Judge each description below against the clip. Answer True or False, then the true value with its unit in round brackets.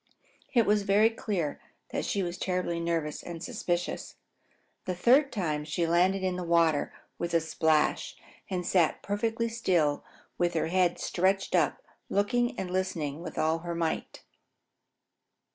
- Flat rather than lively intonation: False (3.2 semitones)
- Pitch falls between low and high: True (180 Hz)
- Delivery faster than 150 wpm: False (145 wpm)